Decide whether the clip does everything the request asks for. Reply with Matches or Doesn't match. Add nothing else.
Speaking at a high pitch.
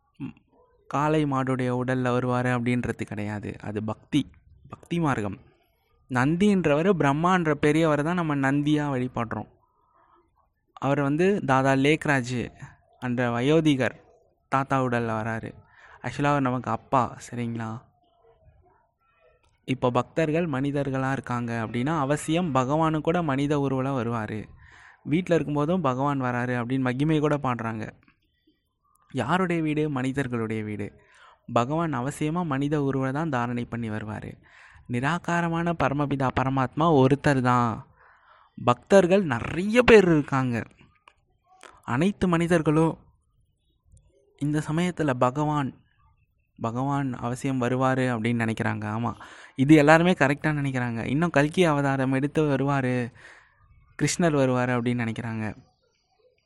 Doesn't match